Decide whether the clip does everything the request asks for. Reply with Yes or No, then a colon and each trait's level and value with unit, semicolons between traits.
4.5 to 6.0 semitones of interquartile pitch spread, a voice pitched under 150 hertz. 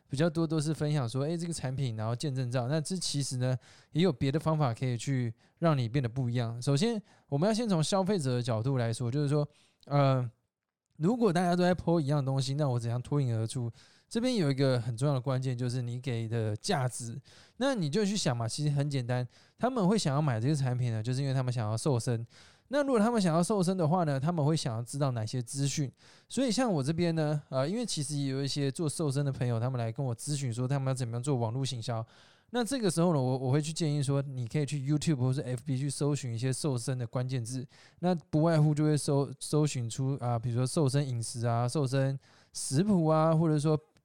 No: average, 3.9 semitones; medium, 140 Hz